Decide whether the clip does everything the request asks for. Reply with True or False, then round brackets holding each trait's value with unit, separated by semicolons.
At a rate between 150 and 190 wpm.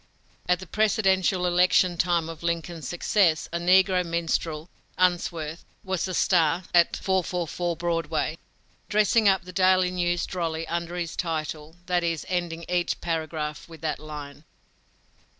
False (135 wpm)